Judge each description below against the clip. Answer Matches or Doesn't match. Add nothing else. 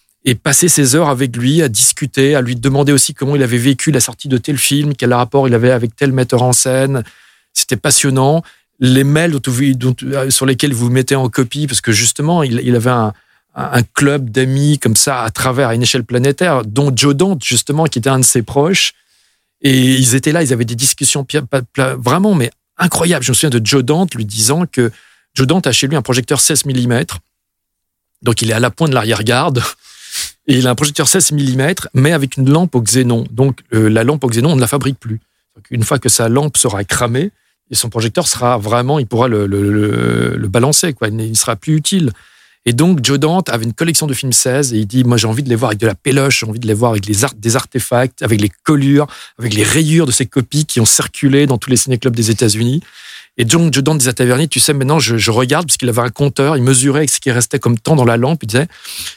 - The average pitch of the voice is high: Doesn't match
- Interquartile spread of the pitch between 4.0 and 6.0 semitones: Doesn't match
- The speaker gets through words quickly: Matches